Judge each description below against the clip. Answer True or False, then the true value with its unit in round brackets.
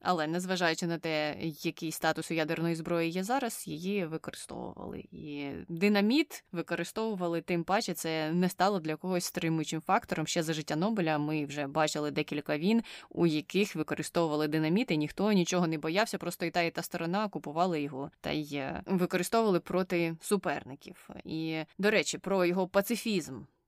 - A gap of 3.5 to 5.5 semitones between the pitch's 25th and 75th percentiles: False (3.0 semitones)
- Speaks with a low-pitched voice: False (170 Hz)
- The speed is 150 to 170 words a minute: True (155 wpm)